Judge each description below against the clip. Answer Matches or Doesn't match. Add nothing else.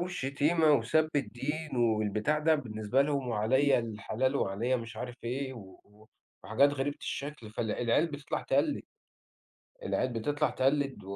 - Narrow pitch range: Doesn't match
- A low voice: Matches